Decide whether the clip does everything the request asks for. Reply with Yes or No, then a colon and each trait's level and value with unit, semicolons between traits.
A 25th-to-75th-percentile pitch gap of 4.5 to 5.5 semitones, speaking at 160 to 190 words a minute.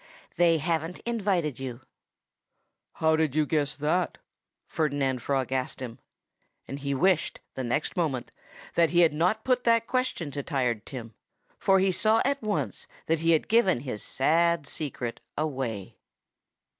No: average, 5.1 semitones; average, 145 wpm